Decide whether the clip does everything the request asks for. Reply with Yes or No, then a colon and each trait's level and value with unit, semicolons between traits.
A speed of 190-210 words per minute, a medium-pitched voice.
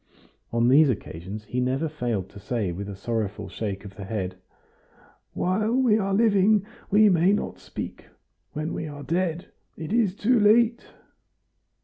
No: average, 155 wpm; medium, 155 Hz